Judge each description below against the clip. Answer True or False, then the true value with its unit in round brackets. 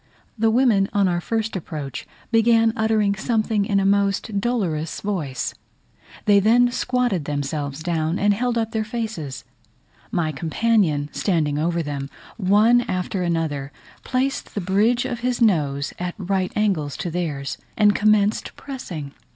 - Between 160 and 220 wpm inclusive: False (145 wpm)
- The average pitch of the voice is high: True (200 Hz)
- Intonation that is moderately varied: False (5.8 semitones)